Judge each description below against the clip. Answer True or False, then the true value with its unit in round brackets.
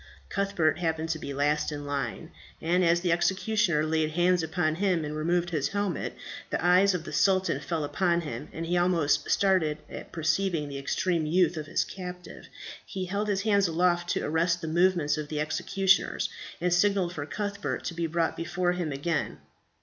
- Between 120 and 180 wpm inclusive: False (190 wpm)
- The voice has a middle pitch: True (170 Hz)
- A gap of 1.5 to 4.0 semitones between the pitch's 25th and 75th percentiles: True (2.8 semitones)